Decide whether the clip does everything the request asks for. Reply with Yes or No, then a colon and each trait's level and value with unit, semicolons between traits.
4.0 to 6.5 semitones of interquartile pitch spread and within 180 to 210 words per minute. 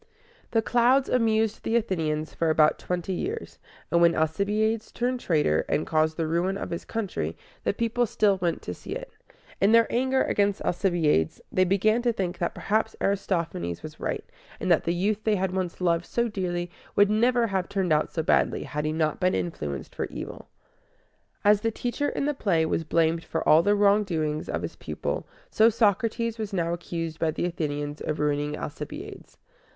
Yes: average, 5.2 semitones; average, 185 wpm